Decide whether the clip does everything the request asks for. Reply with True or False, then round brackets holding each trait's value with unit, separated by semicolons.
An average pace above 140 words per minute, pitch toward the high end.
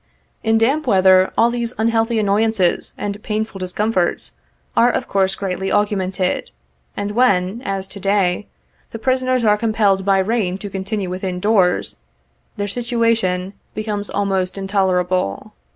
False (135 wpm; 205 Hz)